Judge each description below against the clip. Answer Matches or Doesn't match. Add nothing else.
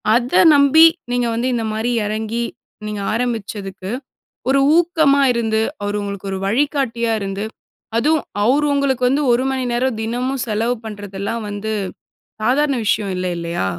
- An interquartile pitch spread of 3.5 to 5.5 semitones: Matches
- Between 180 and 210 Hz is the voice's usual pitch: Doesn't match